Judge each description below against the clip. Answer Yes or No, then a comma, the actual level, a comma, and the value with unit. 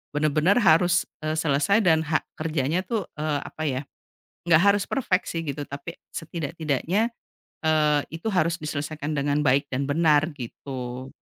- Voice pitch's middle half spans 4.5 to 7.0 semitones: No, average, 2.9 semitones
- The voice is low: No, medium, 155 Hz